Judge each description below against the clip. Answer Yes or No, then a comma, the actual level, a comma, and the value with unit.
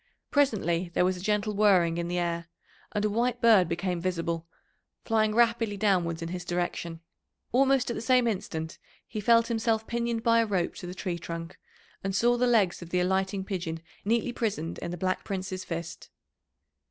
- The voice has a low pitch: No, high, 190 Hz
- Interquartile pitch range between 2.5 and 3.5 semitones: No, average, 4.7 semitones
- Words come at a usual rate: Yes, average, 185 wpm